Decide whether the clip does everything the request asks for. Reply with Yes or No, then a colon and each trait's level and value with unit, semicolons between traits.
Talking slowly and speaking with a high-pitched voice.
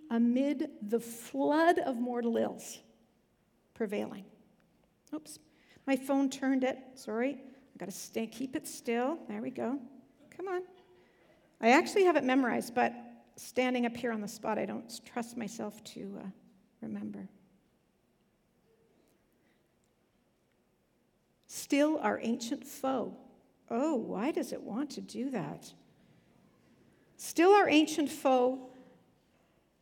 Yes: slow, 120 wpm; very high, 255 Hz